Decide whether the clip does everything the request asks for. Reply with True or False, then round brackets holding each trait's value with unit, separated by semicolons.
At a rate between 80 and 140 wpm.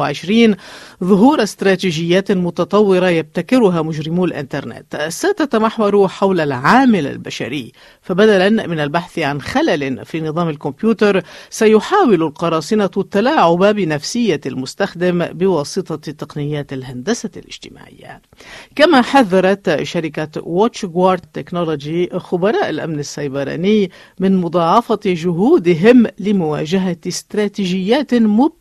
True (85 wpm)